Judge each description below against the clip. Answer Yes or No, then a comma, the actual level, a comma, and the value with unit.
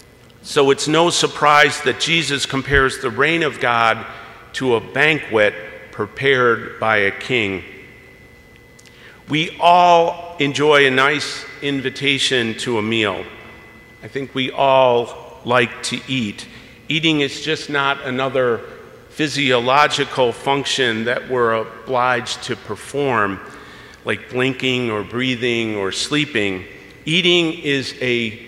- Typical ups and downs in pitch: Yes, average, 3.9 semitones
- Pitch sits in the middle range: No, low, 130 Hz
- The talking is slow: Yes, slow, 115 wpm